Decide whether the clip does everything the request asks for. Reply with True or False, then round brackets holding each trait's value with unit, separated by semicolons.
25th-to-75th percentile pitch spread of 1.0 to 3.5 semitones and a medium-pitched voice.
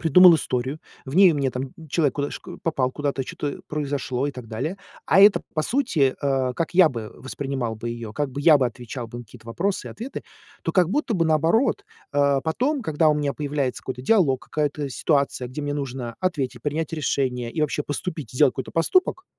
False (4.0 semitones; 145 Hz)